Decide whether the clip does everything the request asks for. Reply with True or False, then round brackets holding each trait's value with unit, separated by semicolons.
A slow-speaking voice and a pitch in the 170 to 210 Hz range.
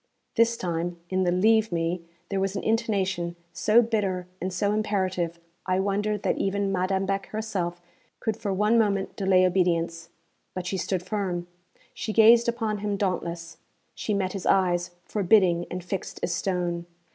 False (165 wpm; 190 Hz)